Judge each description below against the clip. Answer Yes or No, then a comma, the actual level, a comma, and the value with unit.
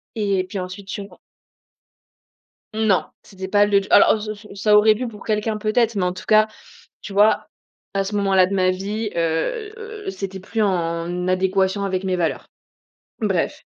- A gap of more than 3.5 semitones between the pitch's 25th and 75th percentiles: No, narrow, 2.4 semitones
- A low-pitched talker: No, high, 195 Hz